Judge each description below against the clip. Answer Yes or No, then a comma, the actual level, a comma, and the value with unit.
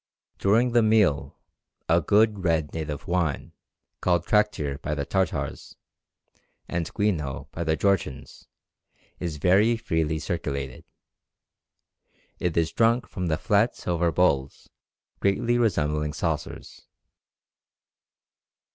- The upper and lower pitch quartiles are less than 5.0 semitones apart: No, average, 5.3 semitones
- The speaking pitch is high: No, very low, 85 Hz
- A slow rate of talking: Yes, slow, 100 wpm